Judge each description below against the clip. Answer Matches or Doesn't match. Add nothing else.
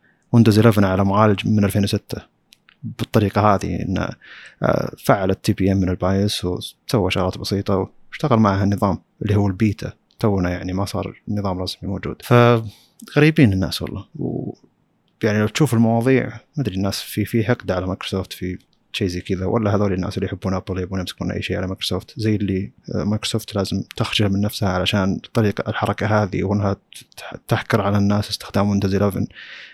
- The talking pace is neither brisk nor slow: Doesn't match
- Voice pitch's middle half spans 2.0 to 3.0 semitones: Matches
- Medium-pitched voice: Doesn't match